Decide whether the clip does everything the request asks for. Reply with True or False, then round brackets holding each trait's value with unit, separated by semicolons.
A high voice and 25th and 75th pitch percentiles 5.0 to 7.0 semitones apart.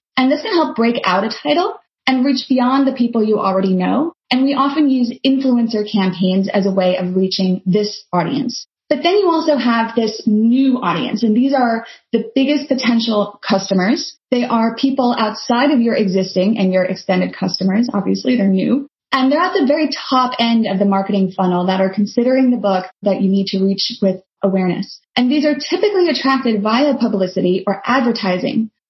True (230 Hz; 5.5 semitones)